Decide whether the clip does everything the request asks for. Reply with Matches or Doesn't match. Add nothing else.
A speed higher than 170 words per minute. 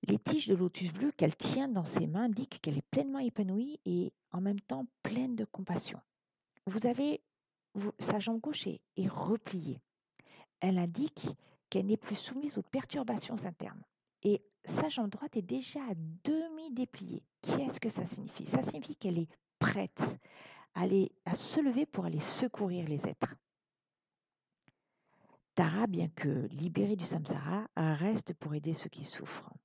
Doesn't match